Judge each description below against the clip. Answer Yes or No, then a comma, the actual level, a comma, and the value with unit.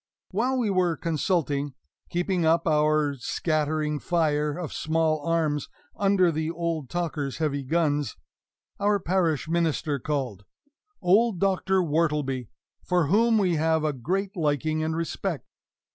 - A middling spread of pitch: Yes, average, 3.0 semitones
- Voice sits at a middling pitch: Yes, medium, 160 Hz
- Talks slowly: Yes, slow, 130 wpm